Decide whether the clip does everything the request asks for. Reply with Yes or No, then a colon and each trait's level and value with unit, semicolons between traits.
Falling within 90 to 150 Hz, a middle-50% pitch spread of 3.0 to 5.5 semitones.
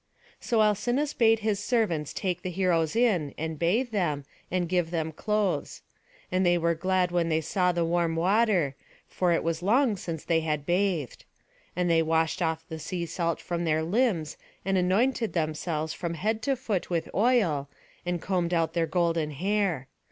No: medium, 175 Hz; average, 3.8 semitones